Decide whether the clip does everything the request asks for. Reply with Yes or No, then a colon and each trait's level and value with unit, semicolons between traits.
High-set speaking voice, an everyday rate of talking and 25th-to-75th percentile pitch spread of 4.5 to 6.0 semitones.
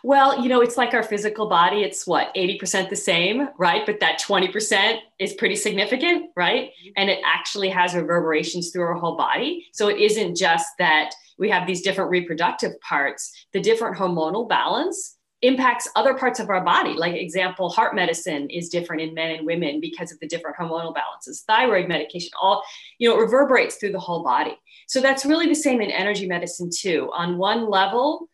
Yes: high, 195 Hz; average, 190 wpm; wide, 5.6 semitones